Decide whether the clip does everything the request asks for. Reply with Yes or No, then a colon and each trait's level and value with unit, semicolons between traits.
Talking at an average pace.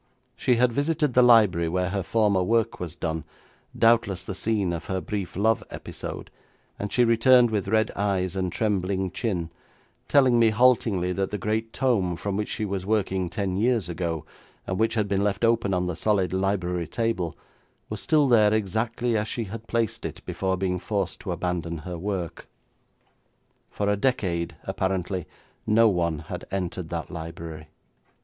Yes: average, 170 wpm